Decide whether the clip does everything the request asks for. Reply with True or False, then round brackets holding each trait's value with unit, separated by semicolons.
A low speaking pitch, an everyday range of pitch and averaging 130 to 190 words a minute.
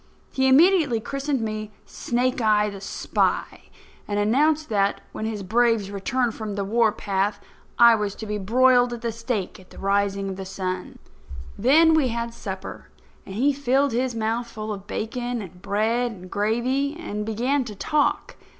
False (225 Hz; 3.7 semitones; 170 wpm)